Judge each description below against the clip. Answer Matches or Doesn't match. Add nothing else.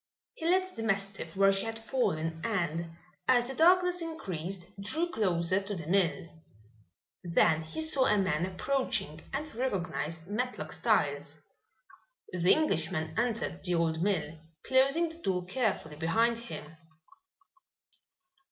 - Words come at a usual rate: Doesn't match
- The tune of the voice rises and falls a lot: Matches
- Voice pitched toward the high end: Matches